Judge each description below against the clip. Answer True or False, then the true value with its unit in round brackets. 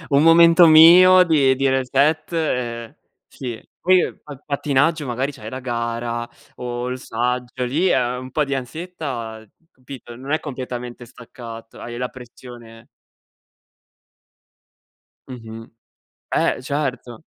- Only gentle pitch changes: False (3.7 semitones)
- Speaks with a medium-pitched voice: False (130 Hz)